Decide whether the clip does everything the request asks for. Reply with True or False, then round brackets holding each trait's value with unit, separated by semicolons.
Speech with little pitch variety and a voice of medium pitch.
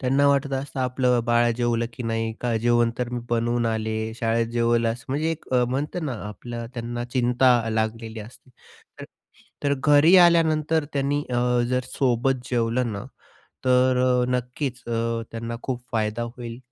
False (2.0 semitones; 120 Hz)